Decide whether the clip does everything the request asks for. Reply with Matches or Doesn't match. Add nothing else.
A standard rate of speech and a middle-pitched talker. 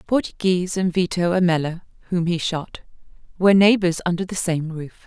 Matches